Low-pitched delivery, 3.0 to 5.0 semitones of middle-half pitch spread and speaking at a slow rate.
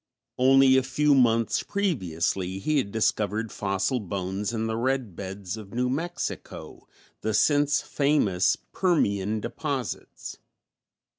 No: low, 115 Hz; wide, 5.5 semitones; slow, 120 wpm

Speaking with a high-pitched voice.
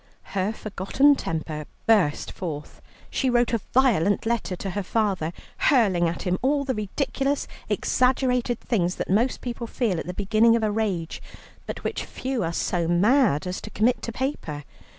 Yes: high, 215 Hz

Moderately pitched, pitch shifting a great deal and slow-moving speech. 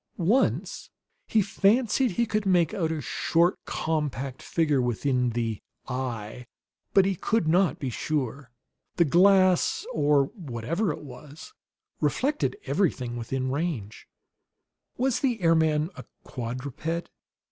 Yes: medium, 155 Hz; wide, 6.7 semitones; slow, 125 wpm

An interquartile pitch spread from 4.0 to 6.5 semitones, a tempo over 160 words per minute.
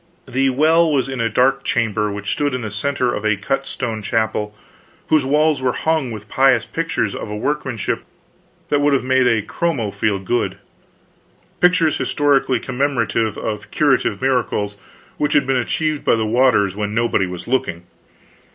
Yes: average, 4.7 semitones; average, 170 wpm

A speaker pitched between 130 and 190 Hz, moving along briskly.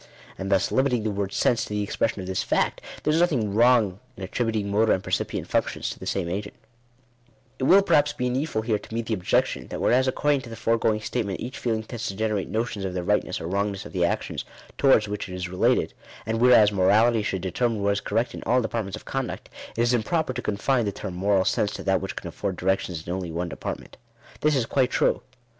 No: low, 110 Hz; fast, 235 wpm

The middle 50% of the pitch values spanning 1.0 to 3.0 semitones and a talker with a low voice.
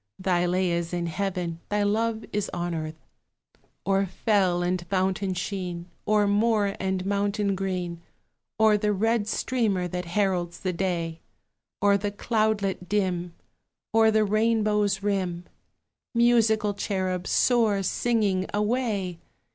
No: average, 2.7 semitones; high, 195 Hz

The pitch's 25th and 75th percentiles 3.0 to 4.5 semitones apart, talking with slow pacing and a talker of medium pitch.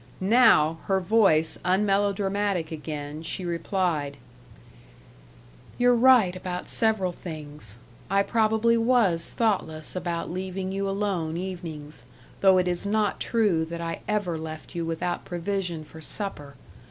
Yes: average, 3.9 semitones; slow, 125 wpm; medium, 180 Hz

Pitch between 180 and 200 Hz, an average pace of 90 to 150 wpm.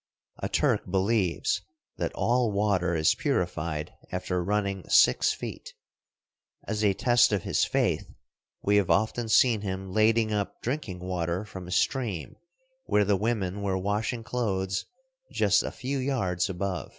No: low, 100 Hz; average, 145 wpm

